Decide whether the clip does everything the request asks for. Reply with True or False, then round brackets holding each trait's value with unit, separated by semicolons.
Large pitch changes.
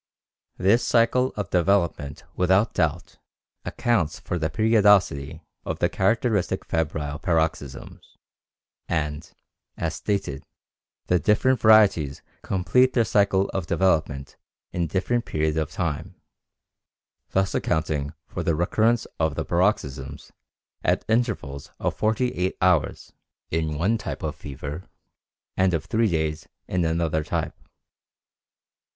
False (4.9 semitones)